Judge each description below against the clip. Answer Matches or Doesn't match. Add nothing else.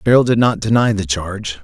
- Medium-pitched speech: Doesn't match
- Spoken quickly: Matches